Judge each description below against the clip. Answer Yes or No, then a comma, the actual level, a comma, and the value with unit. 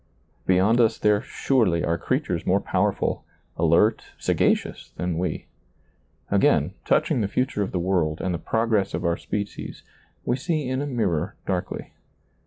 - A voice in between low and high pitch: No, low, 100 Hz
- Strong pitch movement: No, average, 4.7 semitones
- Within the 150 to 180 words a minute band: Yes, average, 155 wpm